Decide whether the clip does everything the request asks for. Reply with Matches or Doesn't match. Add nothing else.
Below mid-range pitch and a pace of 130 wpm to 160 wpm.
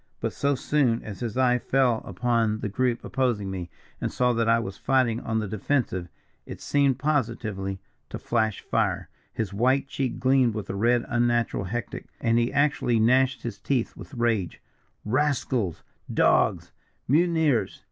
Matches